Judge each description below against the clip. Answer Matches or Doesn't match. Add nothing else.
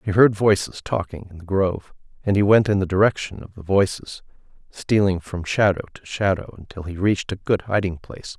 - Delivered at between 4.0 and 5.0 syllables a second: Doesn't match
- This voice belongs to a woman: Doesn't match